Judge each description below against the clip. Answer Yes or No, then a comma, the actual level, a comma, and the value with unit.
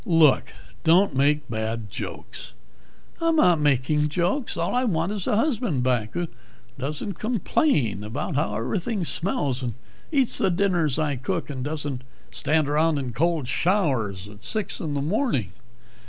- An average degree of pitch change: No, wide, 6.3 semitones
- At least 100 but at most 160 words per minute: Yes, average, 155 wpm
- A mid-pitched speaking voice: Yes, medium, 150 Hz